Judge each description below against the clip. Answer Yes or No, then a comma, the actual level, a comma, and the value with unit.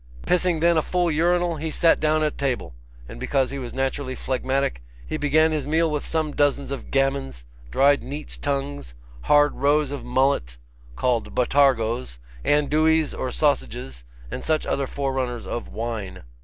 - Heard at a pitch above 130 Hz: Yes, medium, 140 Hz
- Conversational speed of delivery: Yes, average, 155 wpm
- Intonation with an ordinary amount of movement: Yes, average, 3.6 semitones